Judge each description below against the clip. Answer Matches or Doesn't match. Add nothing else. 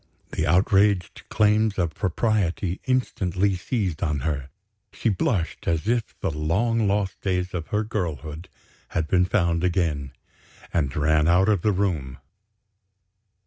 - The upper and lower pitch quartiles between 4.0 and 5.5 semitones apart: Matches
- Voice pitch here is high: Doesn't match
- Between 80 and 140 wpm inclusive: Matches